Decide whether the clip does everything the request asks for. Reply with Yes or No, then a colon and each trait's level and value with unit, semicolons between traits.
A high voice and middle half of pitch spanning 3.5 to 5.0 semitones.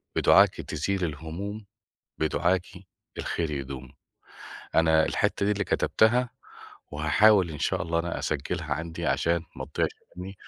No: very low, 85 Hz; average, 3.8 semitones